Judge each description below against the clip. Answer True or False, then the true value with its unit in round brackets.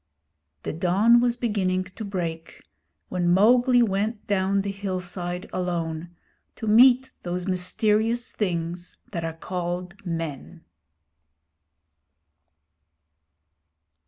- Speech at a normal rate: False (95 wpm)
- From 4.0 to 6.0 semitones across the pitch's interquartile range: False (3.4 semitones)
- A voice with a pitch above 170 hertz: True (185 Hz)